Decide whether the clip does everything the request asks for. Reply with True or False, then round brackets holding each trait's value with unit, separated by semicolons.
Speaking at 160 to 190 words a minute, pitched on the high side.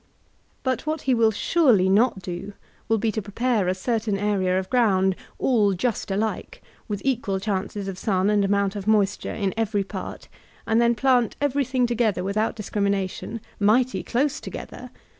True (170 wpm; 210 Hz)